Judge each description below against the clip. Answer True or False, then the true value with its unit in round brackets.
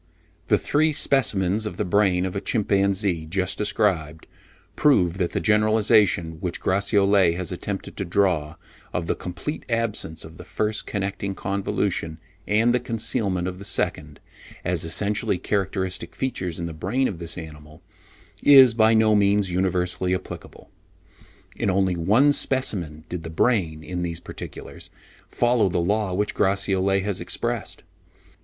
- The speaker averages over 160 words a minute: False (145 wpm)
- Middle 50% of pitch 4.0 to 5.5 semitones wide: False (3.4 semitones)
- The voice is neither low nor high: False (95 Hz)